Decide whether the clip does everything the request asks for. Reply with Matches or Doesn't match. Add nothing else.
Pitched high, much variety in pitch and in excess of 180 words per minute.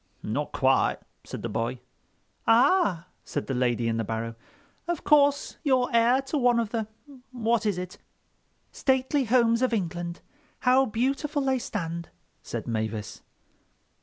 Doesn't match